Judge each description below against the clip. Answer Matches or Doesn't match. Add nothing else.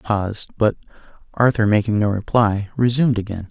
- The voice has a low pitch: Matches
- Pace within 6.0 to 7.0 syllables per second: Matches